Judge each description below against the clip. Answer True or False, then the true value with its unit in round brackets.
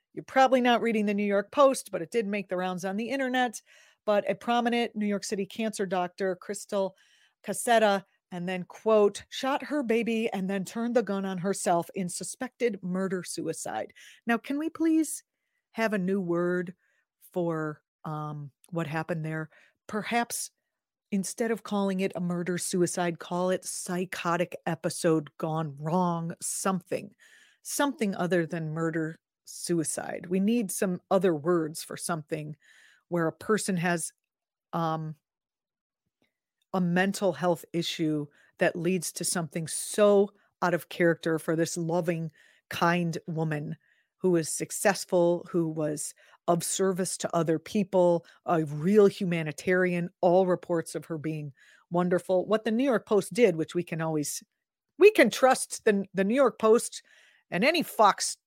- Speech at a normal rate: True (150 wpm)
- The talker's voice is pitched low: False (185 Hz)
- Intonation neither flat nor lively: True (3.9 semitones)